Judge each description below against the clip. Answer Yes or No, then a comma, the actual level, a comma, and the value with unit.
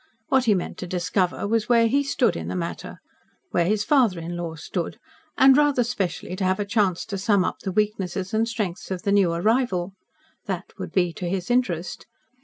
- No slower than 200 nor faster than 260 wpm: Yes, fast, 205 wpm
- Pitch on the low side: No, high, 195 Hz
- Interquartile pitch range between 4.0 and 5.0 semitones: Yes, average, 4.3 semitones